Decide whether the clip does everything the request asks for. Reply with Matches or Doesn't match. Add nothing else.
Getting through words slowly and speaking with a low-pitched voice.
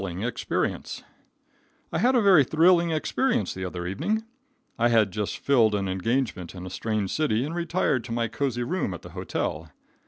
Doesn't match